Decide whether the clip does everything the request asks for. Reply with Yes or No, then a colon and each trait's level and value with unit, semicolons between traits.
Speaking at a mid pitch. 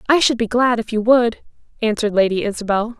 No: high, 225 Hz